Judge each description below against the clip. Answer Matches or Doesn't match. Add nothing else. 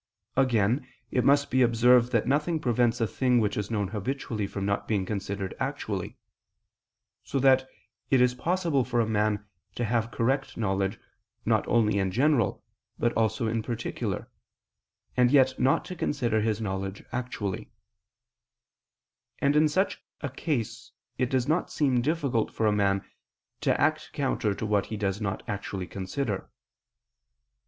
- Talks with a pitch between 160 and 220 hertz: Doesn't match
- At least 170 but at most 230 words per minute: Doesn't match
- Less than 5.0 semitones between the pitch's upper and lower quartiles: Matches